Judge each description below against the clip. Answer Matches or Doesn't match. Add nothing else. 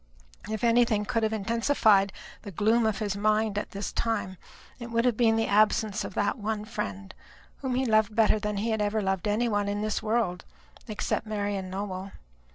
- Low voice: Doesn't match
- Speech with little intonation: Matches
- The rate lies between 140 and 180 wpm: Doesn't match